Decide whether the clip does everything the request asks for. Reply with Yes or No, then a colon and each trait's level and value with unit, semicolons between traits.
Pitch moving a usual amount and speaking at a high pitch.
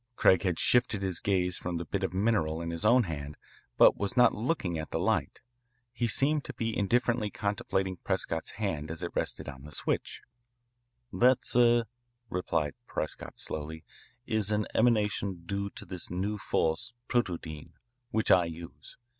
No: average, 4.9 semitones; very low, 95 Hz